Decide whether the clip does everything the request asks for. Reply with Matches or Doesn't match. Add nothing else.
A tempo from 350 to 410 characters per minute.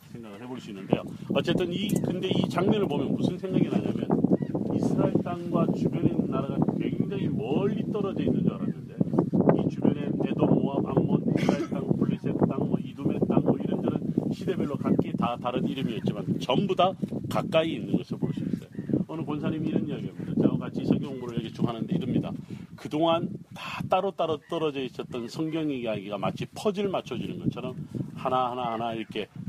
Matches